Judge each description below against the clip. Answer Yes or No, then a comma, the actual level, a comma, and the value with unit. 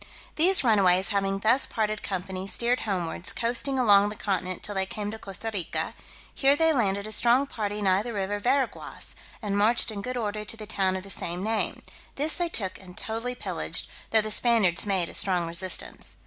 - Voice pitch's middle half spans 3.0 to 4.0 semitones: Yes, average, 3.5 semitones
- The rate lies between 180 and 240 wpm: Yes, average, 195 wpm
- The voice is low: No, high, 210 Hz